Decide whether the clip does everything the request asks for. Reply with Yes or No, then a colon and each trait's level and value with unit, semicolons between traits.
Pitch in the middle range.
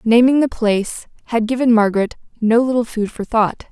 No: high, 230 Hz